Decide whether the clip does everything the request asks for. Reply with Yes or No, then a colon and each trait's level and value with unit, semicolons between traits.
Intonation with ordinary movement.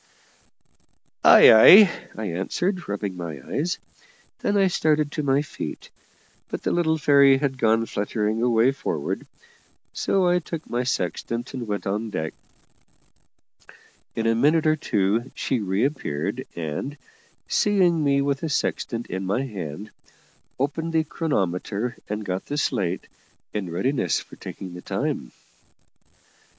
No: wide, 7.0 semitones